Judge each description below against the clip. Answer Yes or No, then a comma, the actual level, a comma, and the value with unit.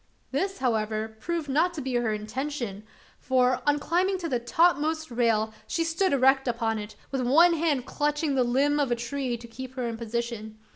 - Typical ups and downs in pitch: Yes, average, 4.1 semitones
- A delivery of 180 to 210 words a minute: Yes, average, 190 wpm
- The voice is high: Yes, very high, 260 Hz